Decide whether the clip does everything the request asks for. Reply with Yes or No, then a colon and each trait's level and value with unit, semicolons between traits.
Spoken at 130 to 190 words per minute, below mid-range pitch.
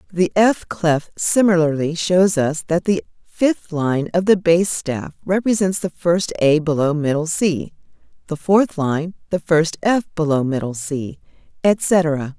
No: average, 150 wpm; medium, 170 Hz